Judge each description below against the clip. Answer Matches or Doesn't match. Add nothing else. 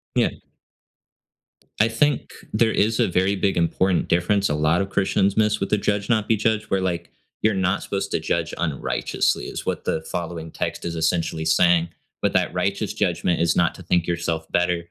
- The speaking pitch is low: Matches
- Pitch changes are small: Doesn't match